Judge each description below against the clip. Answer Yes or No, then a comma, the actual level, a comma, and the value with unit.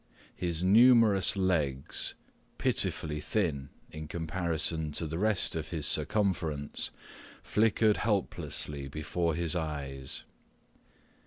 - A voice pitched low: Yes, very low, 80 Hz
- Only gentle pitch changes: No, average, 4.3 semitones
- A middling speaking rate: No, slow, 95 wpm